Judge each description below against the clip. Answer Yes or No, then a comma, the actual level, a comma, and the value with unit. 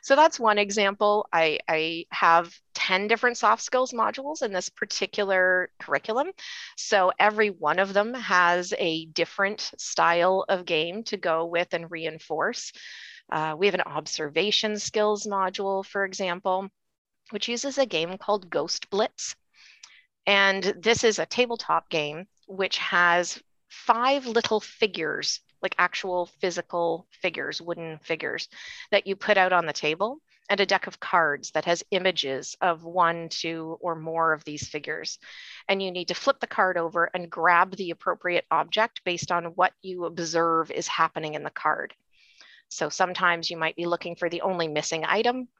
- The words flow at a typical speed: Yes, average, 160 wpm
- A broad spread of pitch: No, average, 3.8 semitones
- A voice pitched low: No, medium, 185 Hz